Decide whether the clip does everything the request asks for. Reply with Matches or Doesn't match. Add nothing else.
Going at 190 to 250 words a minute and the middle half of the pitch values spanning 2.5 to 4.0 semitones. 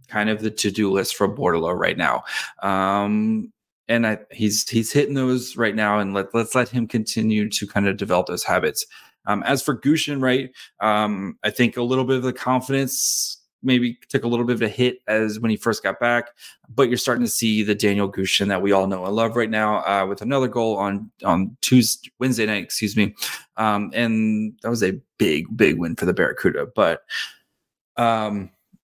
Matches